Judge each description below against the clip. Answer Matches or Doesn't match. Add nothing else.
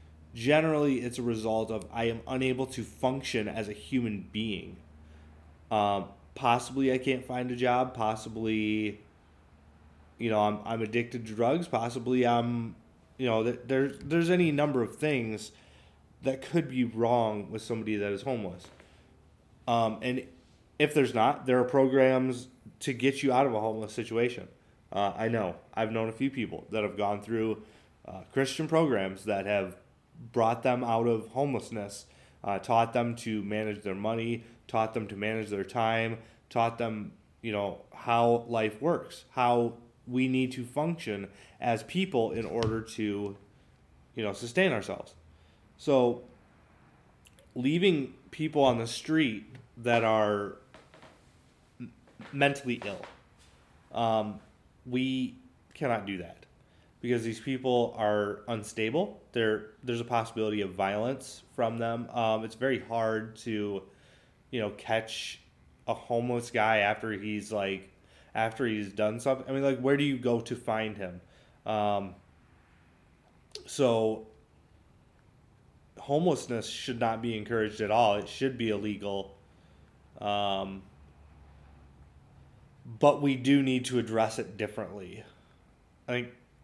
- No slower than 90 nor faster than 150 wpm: Matches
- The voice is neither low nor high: Doesn't match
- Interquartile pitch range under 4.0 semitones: Matches